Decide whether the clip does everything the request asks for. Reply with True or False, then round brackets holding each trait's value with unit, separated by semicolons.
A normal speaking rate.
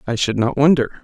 False (230 wpm)